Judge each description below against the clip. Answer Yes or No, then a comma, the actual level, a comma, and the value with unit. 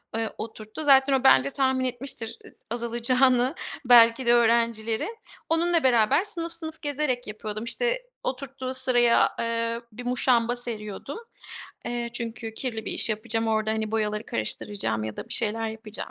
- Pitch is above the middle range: Yes, high, 235 Hz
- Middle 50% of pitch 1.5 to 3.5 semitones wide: Yes, average, 3.0 semitones